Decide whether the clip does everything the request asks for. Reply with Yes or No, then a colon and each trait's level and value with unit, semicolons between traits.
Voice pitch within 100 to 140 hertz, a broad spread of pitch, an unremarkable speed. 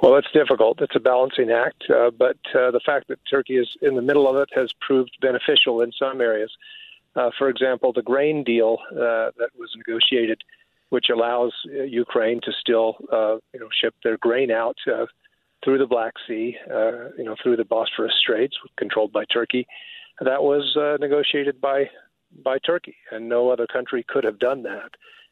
No: low, 135 Hz; average, 4.3 semitones; average, 185 wpm